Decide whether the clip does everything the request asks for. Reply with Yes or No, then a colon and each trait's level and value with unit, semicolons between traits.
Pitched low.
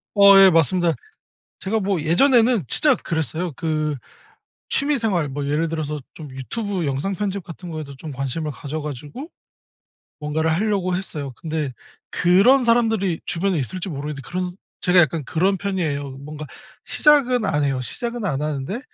No: medium, 165 Hz